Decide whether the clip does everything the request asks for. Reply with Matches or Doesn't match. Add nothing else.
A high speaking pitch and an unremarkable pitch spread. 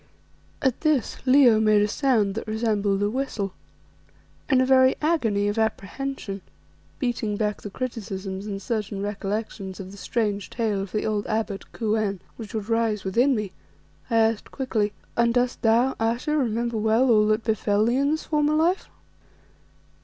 Matches